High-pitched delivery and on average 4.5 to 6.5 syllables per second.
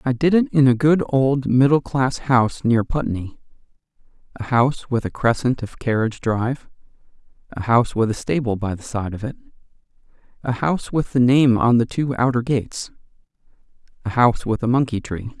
No: low, 125 Hz; 5.5 syllables/s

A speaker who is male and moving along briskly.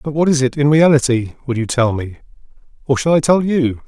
Yes: male; fast, 230 wpm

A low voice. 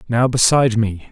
Yes: low, 115 Hz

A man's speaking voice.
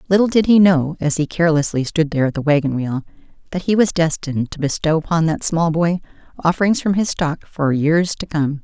No: female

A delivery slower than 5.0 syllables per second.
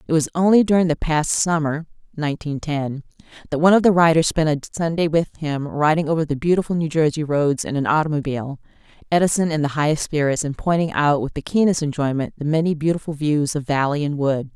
No: 6.0 syllables/s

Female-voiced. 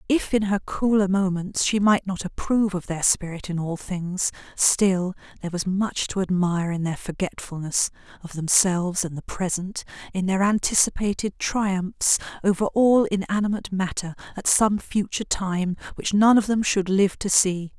Yes: female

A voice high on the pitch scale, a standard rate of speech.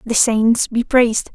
Yes: high, 235 Hz; average, 180 wpm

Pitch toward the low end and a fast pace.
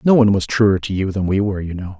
Yes: low, 100 Hz; fast, 330 wpm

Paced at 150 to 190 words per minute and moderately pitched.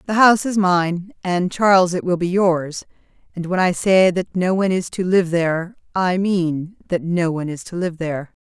No: average, 200 wpm; medium, 180 Hz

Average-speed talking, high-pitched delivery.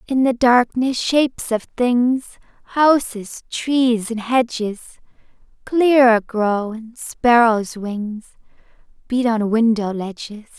No: slow, 110 wpm; high, 235 Hz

